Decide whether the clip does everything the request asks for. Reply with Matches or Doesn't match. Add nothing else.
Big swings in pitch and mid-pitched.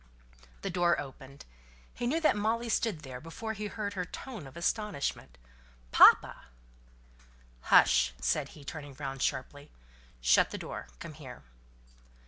Matches